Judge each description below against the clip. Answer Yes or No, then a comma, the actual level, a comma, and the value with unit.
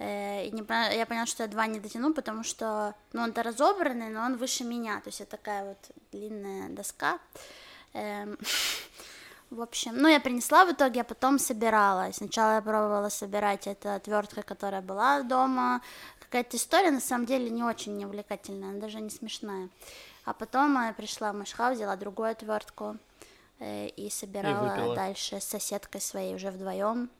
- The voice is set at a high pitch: Yes, high, 215 Hz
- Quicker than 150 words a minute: Yes, fast, 160 wpm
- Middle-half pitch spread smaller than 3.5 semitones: Yes, average, 3.1 semitones